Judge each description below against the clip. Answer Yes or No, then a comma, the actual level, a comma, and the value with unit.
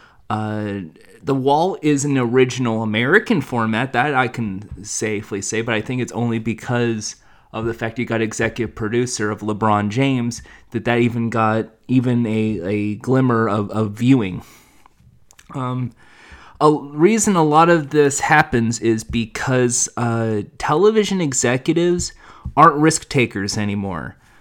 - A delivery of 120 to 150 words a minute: Yes, average, 140 wpm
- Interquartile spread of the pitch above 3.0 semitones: Yes, average, 3.4 semitones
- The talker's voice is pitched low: Yes, low, 120 Hz